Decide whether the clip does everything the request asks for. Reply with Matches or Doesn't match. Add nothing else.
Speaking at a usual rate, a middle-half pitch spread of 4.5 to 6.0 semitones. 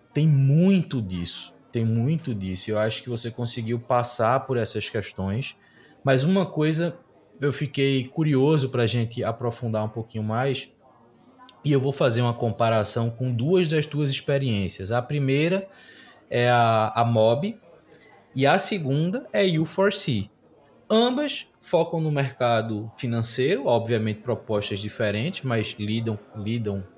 Matches